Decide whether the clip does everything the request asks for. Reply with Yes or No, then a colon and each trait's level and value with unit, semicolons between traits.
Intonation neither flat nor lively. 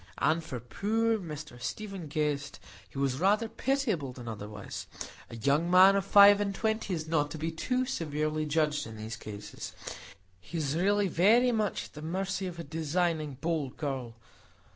No: wide, 5.9 semitones